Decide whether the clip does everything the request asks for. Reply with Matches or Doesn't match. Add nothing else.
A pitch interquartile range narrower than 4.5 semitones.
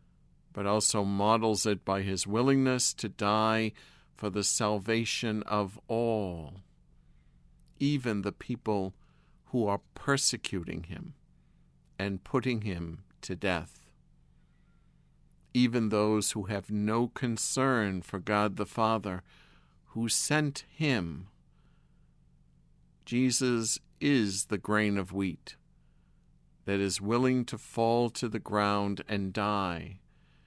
Matches